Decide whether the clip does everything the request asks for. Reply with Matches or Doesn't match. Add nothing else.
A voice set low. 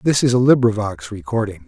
Matches